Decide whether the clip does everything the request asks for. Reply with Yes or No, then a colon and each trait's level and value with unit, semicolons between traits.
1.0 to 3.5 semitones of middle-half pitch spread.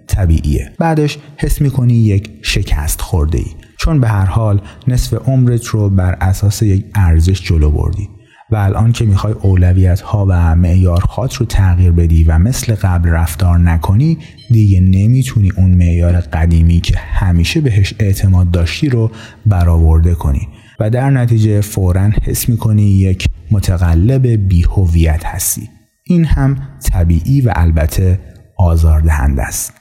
No: average, 4.6 semitones